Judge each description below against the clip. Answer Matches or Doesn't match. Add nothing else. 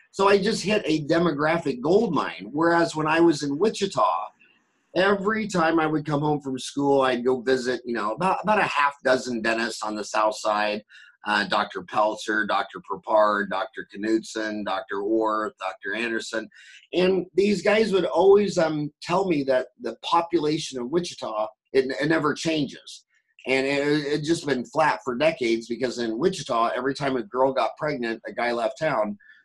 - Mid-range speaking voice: Matches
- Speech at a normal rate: Matches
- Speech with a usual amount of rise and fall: Doesn't match